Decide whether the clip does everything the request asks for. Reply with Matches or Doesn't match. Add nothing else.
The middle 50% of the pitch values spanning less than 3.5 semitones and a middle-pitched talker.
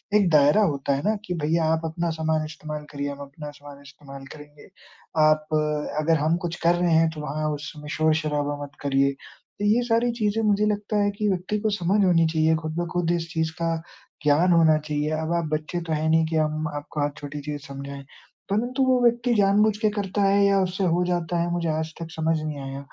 Doesn't match